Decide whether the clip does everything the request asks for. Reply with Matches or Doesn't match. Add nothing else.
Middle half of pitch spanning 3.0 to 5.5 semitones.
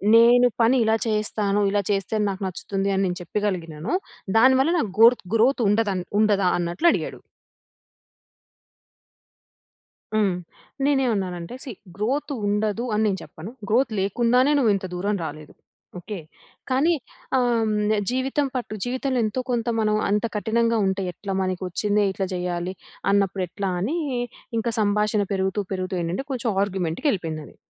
Matches